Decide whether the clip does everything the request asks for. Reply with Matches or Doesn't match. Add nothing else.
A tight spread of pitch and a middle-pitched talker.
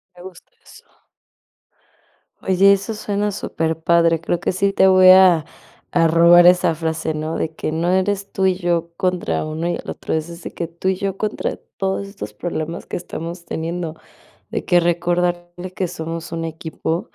Matches